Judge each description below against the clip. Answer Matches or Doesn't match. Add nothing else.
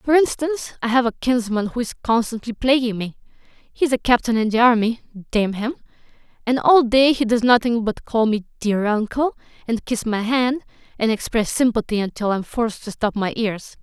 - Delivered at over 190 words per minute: Matches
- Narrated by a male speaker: Doesn't match